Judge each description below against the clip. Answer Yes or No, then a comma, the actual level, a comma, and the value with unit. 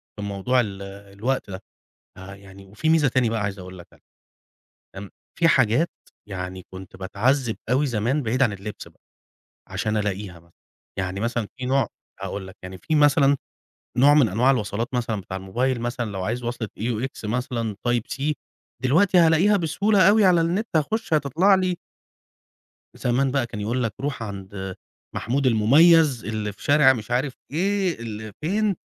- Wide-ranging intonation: Yes, wide, 6.2 semitones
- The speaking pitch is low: Yes, low, 120 Hz